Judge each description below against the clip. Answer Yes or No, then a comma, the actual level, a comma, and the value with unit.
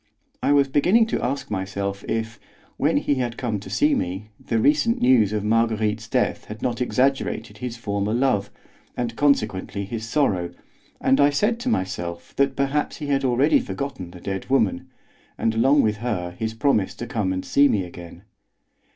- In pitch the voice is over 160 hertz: No, low, 115 Hz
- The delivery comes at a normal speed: Yes, average, 175 wpm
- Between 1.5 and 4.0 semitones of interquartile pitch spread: No, average, 5.3 semitones